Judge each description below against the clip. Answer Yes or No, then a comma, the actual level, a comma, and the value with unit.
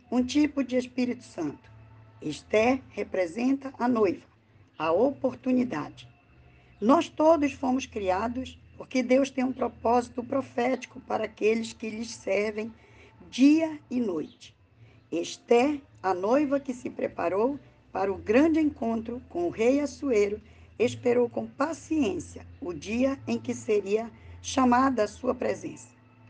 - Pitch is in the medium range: No, high, 245 Hz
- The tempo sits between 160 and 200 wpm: No, average, 125 wpm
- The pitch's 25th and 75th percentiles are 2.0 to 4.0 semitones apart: No, average, 4.5 semitones